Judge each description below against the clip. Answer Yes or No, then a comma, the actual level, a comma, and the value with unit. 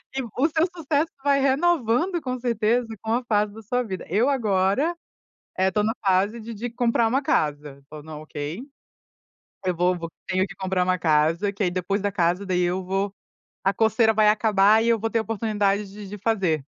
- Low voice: No, high, 210 Hz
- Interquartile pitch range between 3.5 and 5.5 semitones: Yes, average, 4.0 semitones